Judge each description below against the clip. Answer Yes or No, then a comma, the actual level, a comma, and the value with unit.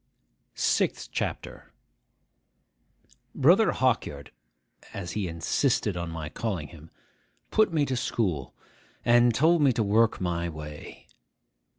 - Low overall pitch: Yes, low, 100 Hz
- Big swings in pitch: Yes, wide, 6.5 semitones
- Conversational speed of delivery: No, slow, 110 wpm